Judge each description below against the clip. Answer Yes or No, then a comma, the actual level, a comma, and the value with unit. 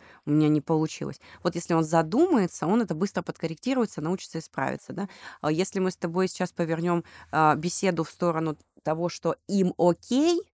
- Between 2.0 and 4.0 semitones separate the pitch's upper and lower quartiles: Yes, average, 2.8 semitones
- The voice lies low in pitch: No, medium, 175 Hz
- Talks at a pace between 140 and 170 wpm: Yes, fast, 160 wpm